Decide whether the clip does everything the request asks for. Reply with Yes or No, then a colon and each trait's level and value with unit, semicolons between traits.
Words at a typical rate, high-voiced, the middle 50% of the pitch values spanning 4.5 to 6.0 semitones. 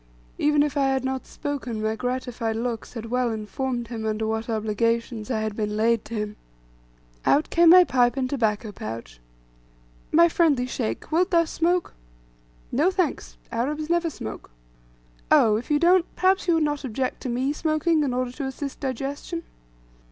Yes: average, 170 wpm; very high, 255 Hz; average, 5.2 semitones